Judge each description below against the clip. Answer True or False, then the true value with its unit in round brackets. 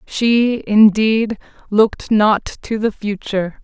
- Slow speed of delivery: True (115 wpm)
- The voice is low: False (215 Hz)